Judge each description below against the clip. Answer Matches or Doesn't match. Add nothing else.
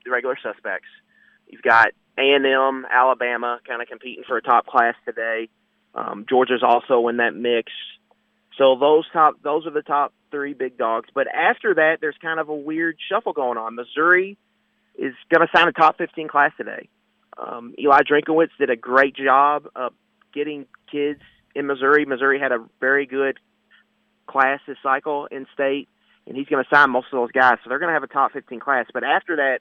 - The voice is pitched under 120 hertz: Doesn't match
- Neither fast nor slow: Matches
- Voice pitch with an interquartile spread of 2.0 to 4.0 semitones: Matches